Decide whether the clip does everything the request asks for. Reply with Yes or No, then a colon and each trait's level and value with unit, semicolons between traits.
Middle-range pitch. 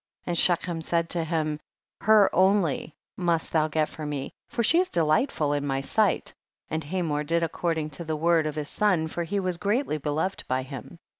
Yes: medium, 165 Hz